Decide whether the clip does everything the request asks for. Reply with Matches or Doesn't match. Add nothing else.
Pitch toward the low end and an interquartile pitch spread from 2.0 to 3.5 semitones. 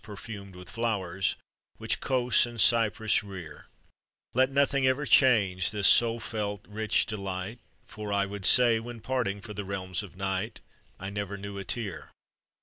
Matches